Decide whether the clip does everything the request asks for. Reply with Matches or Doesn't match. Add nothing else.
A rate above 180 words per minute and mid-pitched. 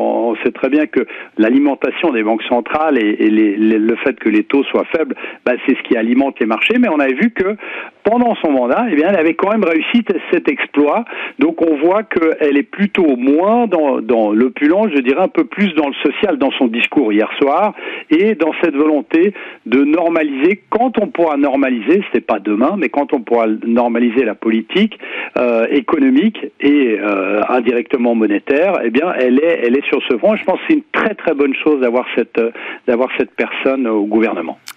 Matches